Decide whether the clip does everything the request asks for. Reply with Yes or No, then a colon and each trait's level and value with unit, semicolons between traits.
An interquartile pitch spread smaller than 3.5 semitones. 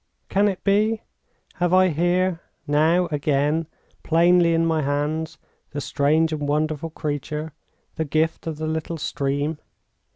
Yes: narrow, 2.4 semitones